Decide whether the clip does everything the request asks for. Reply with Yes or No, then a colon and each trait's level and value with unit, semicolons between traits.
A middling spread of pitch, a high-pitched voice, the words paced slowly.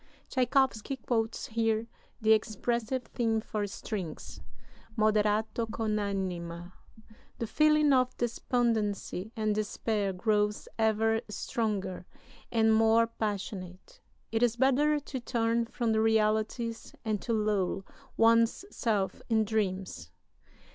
No: narrow, 2.0 semitones; high, 220 Hz; slow, 110 wpm